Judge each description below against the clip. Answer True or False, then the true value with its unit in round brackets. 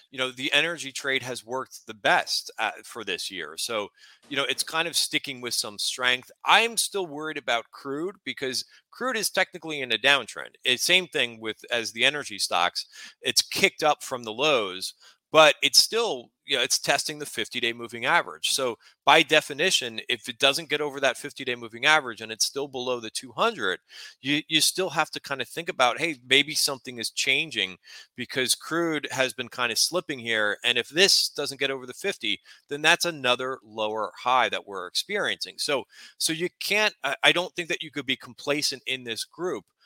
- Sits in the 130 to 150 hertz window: True (135 Hz)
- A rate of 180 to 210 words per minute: True (200 wpm)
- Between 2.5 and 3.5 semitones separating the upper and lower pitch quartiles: False (4.0 semitones)